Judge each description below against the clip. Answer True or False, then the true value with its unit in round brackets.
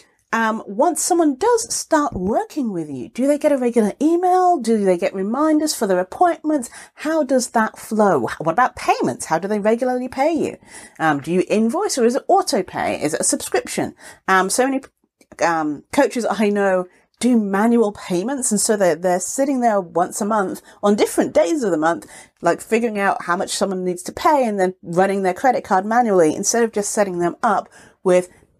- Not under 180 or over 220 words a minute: True (200 wpm)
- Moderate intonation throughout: False (7.1 semitones)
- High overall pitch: True (220 Hz)